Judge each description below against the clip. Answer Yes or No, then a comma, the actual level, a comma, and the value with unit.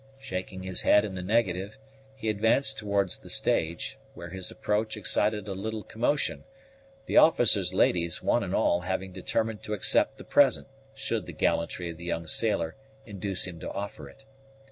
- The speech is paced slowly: No, average, 170 wpm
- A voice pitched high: No, low, 100 Hz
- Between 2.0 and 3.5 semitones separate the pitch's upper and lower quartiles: Yes, average, 3.1 semitones